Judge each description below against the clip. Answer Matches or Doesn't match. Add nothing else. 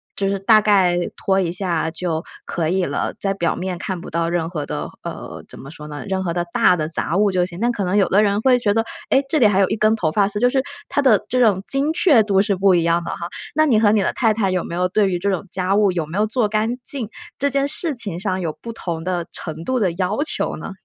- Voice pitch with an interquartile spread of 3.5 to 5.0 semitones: Matches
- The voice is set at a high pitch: Matches